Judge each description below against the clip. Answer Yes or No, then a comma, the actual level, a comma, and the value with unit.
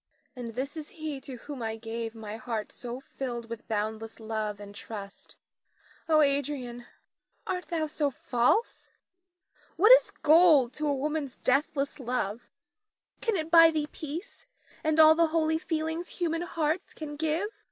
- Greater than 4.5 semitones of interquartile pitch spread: Yes, average, 5.2 semitones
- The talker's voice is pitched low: No, very high, 285 Hz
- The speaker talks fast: No, average, 155 wpm